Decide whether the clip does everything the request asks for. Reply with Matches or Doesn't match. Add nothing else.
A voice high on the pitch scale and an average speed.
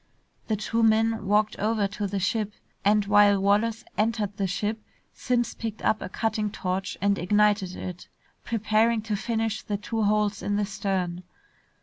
Matches